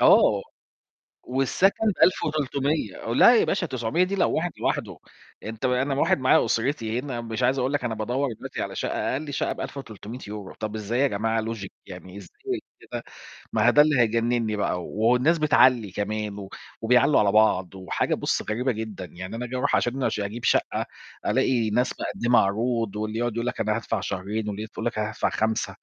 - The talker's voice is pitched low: Yes, low, 115 Hz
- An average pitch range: Yes, average, 3.6 semitones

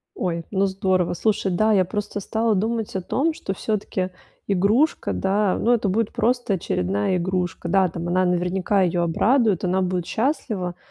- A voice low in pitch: No, high, 190 Hz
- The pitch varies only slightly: No, average, 3.3 semitones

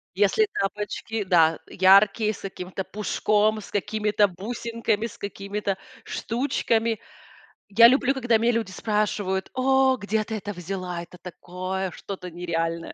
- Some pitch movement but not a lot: Yes, average, 3.1 semitones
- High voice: Yes, high, 205 Hz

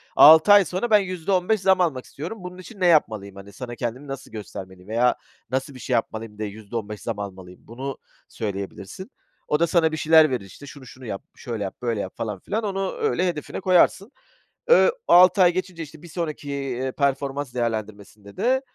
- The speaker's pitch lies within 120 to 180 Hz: Yes, low, 135 Hz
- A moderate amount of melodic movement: No, wide, 8.3 semitones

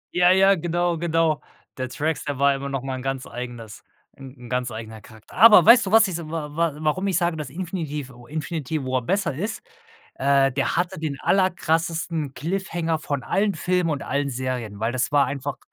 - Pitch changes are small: No, average, 4.6 semitones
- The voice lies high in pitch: No, medium, 150 Hz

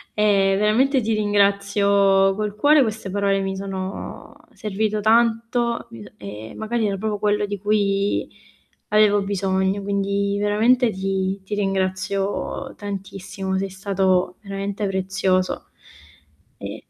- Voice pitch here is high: Yes, high, 200 Hz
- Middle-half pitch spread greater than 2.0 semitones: No, narrow, 1.6 semitones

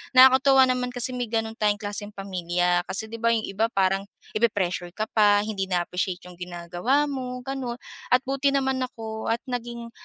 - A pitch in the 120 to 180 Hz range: No, high, 220 Hz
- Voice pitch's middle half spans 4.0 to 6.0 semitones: Yes, average, 4.5 semitones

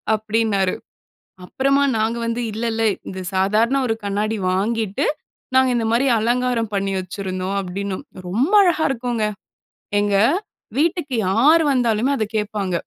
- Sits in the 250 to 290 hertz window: No, high, 220 Hz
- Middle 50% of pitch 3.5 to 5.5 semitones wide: Yes, average, 3.8 semitones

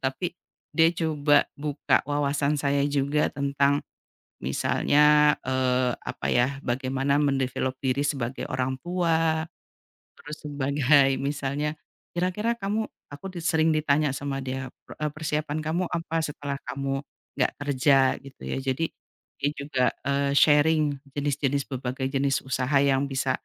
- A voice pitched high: No, medium, 140 Hz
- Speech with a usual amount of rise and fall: No, narrow, 2.0 semitones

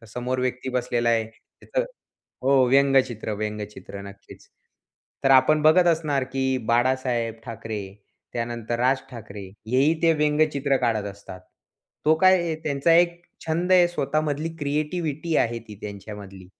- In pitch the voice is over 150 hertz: No, low, 130 Hz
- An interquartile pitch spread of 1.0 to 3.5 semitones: No, average, 5.1 semitones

